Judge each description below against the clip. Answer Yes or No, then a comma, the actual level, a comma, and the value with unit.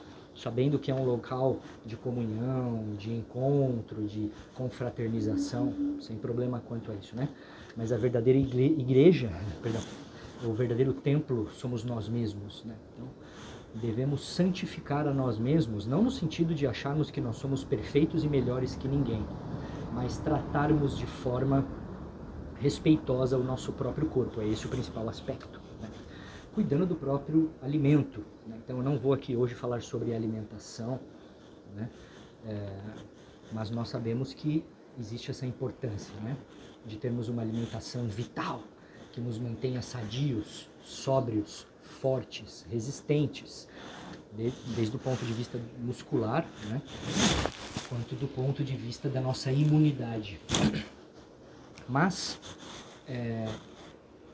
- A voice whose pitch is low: Yes, low, 125 Hz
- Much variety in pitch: No, average, 3.7 semitones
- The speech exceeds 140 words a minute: No, average, 130 wpm